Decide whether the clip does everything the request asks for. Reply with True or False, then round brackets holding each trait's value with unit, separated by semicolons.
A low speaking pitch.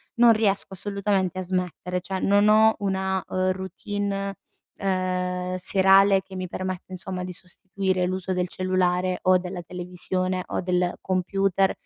False (185 Hz)